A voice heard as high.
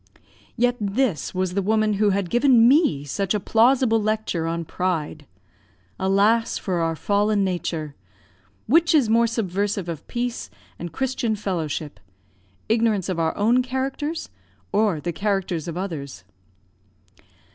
Yes: high, 200 Hz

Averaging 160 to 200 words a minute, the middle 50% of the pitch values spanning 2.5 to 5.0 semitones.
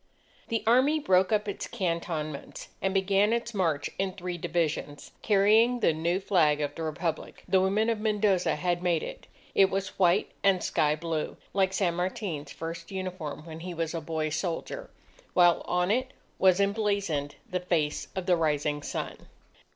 Yes: average, 165 wpm; average, 3.4 semitones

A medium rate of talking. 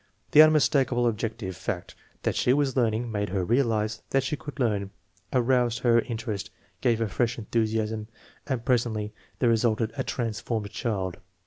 Yes: average, 155 wpm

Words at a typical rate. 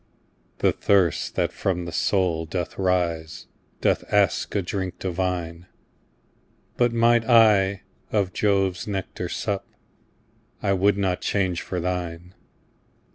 No: slow, 120 wpm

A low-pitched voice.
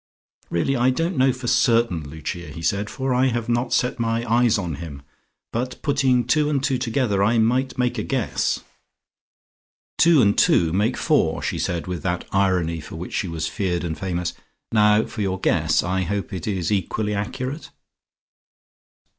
Yes: low, 105 Hz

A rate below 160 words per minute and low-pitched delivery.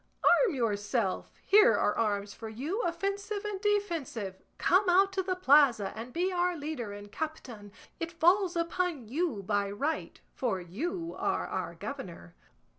No: average, 150 wpm; very high, 310 Hz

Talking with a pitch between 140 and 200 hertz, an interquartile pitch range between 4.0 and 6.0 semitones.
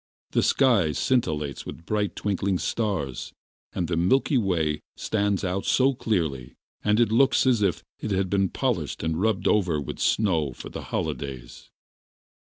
No: very low, 95 Hz; average, 5.3 semitones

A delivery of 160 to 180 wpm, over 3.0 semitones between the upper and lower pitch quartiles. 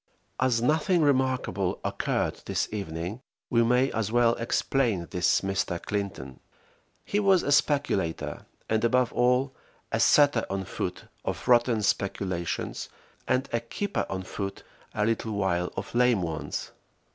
No: slow, 135 wpm; average, 4.8 semitones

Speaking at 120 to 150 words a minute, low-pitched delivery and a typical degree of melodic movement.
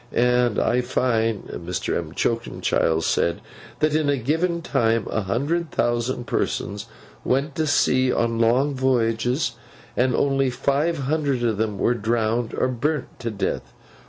Yes: average, 140 wpm; low, 125 Hz; average, 3.6 semitones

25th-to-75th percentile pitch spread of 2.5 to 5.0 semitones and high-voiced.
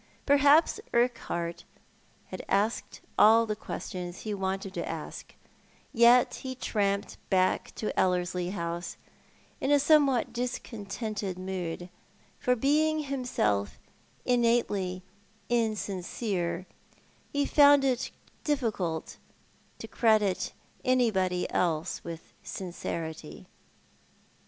No: wide, 5.6 semitones; high, 210 Hz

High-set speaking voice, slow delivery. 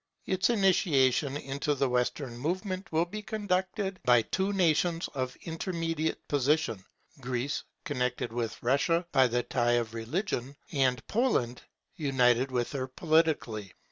No: medium, 140 Hz; slow, 130 wpm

